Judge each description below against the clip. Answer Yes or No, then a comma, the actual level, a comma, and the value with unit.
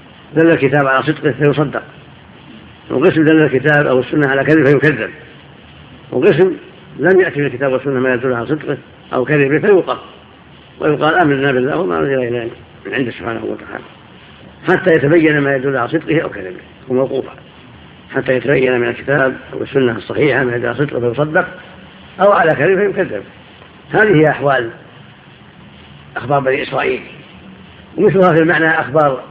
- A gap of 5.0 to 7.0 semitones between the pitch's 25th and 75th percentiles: No, average, 3.6 semitones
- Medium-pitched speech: Yes, medium, 145 Hz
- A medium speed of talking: No, fast, 145 wpm